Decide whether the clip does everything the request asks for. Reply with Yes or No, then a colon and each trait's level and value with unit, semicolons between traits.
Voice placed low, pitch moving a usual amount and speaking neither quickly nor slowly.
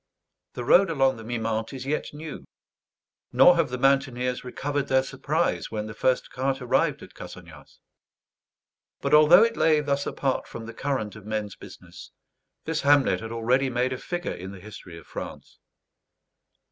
Yes: low, 130 Hz; average, 4.1 semitones; average, 165 wpm